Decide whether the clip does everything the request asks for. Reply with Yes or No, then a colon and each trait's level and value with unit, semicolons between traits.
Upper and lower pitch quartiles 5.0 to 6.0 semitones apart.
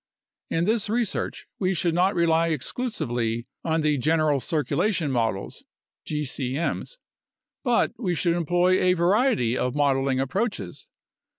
Yes: wide, 5.4 semitones